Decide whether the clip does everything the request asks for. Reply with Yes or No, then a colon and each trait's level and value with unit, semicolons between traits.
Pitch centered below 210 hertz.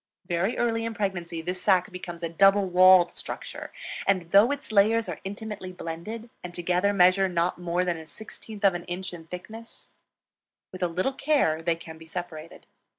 Yes: medium, 185 Hz